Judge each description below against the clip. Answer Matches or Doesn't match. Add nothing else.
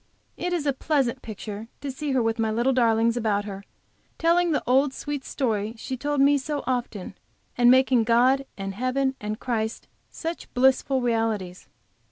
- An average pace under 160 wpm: Doesn't match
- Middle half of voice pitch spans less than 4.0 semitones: Matches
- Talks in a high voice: Matches